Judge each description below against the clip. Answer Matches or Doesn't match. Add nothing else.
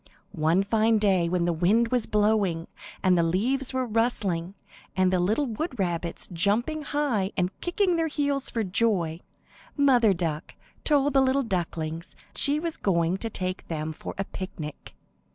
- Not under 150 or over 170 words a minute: Matches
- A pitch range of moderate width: Doesn't match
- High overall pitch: Matches